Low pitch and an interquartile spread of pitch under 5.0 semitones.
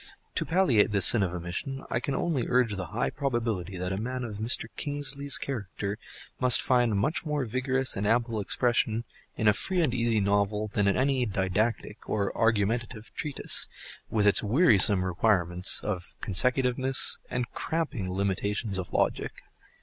Yes: low, 115 Hz; average, 4.3 semitones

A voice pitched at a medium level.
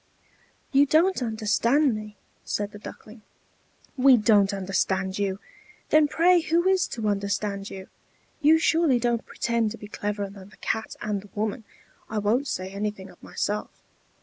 No: high, 215 Hz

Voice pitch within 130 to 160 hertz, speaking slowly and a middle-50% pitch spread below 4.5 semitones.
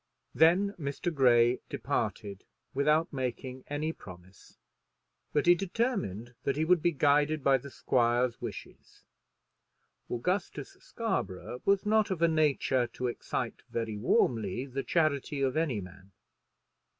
No: medium, 140 Hz; slow, 125 wpm; average, 5.3 semitones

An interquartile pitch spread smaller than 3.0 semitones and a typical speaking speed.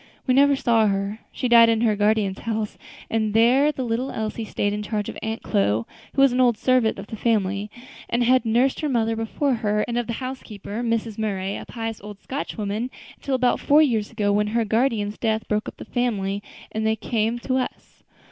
No: narrow, 2.6 semitones; fast, 215 wpm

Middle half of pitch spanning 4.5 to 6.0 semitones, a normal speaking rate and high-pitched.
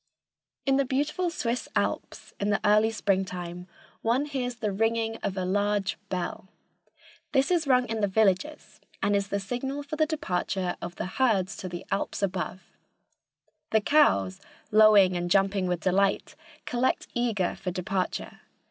Yes: average, 4.8 semitones; average, 155 wpm; high, 205 Hz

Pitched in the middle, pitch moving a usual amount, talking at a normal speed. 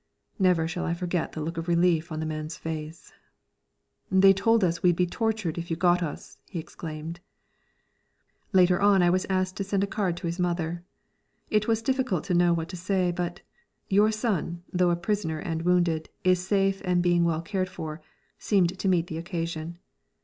No: medium, 175 Hz; narrow, 2.3 semitones; average, 190 wpm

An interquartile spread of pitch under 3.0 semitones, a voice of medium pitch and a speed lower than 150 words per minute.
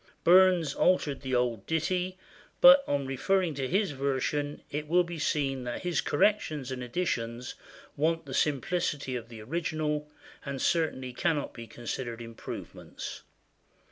No: average, 4.9 semitones; medium, 145 Hz; average, 140 wpm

